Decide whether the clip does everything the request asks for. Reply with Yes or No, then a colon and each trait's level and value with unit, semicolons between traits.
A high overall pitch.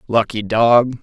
No: low, 115 Hz